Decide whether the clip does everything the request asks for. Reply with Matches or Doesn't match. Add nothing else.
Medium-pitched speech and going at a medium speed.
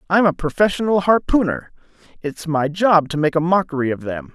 Matches